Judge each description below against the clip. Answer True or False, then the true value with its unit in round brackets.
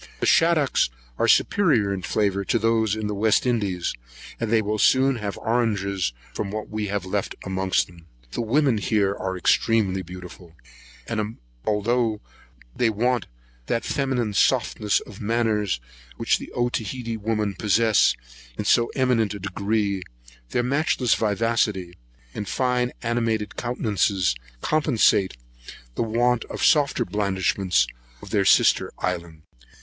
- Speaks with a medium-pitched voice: False (110 Hz)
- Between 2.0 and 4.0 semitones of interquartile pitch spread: True (3.1 semitones)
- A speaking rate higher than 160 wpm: False (135 wpm)